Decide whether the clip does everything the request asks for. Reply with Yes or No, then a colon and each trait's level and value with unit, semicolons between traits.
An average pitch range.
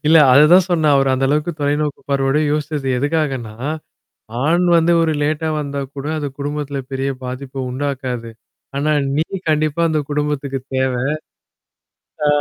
No: narrow, 2.1 semitones